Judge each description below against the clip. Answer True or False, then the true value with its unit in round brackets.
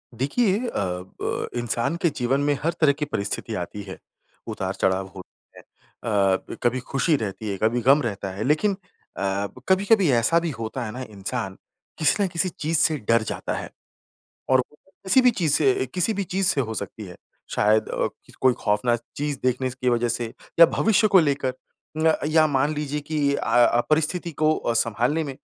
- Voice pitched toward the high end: False (135 Hz)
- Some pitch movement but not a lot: False (5.8 semitones)